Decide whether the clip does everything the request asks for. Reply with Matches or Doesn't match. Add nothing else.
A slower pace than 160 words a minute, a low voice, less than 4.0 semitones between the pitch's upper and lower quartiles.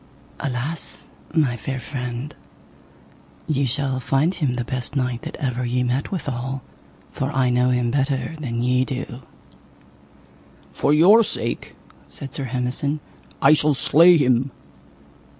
Matches